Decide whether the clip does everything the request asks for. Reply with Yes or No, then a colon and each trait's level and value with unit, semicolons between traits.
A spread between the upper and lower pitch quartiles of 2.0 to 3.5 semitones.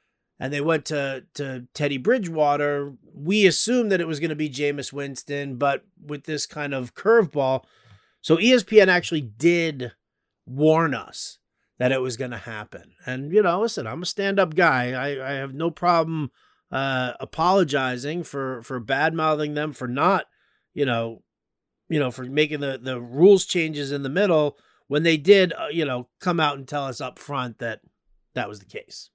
No: average, 4.0 semitones